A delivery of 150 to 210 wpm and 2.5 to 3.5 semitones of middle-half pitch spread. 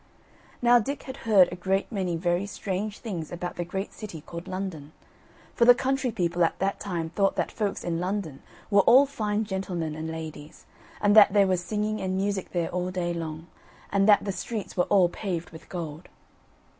Yes: average, 195 wpm; average, 3.2 semitones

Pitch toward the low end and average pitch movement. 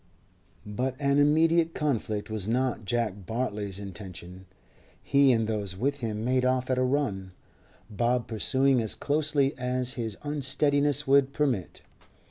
Yes: low, 125 Hz; average, 4.6 semitones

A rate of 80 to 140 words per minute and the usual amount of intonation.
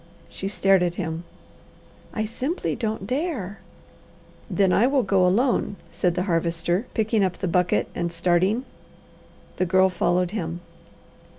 Yes: slow, 135 wpm; average, 3.7 semitones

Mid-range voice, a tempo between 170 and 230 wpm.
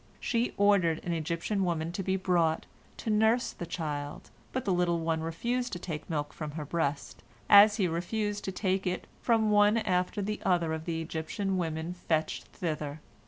Yes: medium, 175 Hz; average, 180 wpm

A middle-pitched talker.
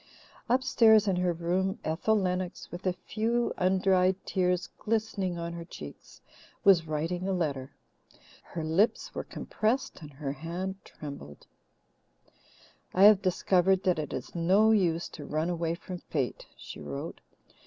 Yes: medium, 180 Hz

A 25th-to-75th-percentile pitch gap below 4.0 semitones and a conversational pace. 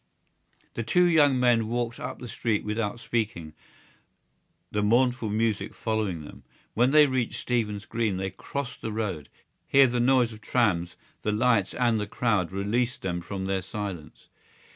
Yes: average, 3.3 semitones; average, 160 wpm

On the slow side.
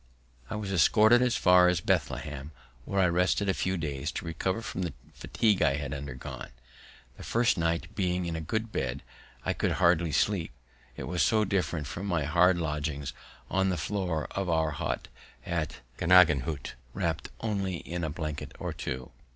No: average, 175 wpm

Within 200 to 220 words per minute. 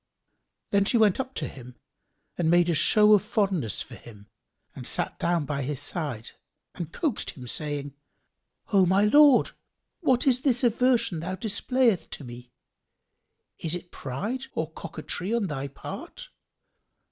No: average, 150 wpm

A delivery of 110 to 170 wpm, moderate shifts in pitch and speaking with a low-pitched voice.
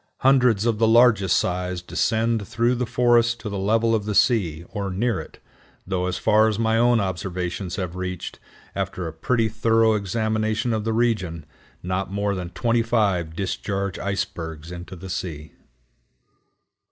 Yes: average, 160 wpm; average, 3.7 semitones; low, 105 Hz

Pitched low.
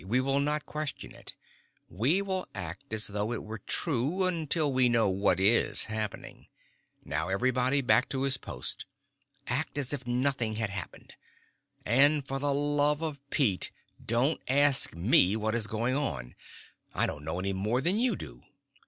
Yes: low, 125 Hz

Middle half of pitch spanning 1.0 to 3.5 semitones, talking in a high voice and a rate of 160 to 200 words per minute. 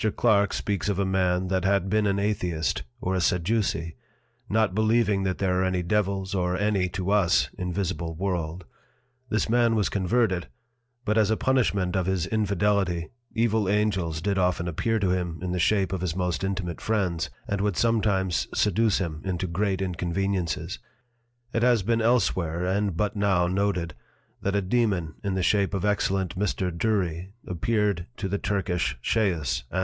No: narrow, 2.6 semitones; very low, 95 Hz; average, 170 wpm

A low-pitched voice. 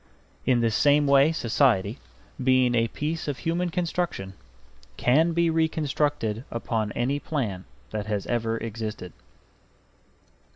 Yes: low, 130 Hz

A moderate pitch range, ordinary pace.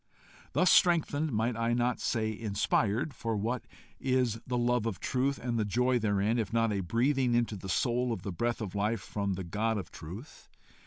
Yes: average, 3.0 semitones; average, 195 wpm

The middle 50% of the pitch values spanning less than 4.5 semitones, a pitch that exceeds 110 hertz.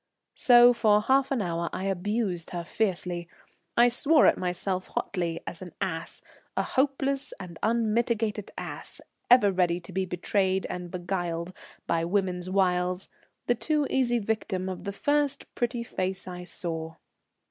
No: average, 4.8 semitones; high, 190 Hz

